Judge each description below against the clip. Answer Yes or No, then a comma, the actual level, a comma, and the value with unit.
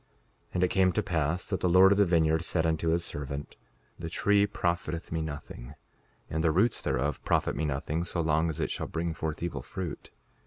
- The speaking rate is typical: No, fast, 210 wpm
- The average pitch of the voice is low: Yes, very low, 80 Hz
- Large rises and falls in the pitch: No, narrow, 2.6 semitones